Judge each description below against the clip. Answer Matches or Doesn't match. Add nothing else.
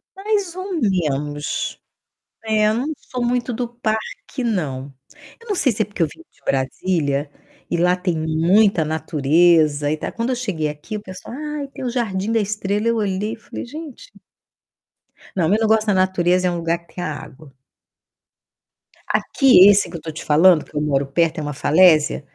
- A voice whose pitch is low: Doesn't match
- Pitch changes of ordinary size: Doesn't match